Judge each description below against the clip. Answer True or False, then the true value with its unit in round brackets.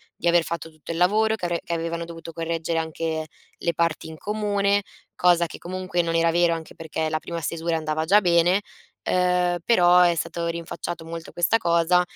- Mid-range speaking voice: True (170 Hz)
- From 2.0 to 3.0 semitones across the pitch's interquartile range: False (1.4 semitones)